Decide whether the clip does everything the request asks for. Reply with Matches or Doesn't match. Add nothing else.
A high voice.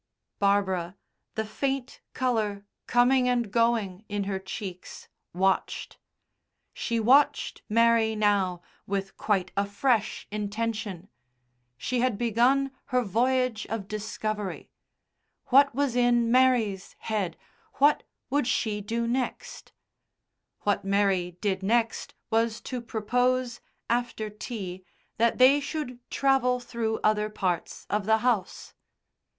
Matches